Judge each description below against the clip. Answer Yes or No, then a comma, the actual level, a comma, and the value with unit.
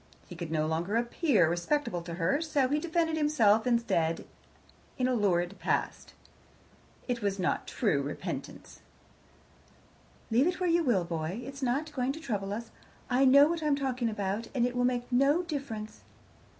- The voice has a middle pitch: No, high, 245 Hz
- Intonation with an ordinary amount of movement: No, wide, 6.3 semitones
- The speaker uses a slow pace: No, average, 165 wpm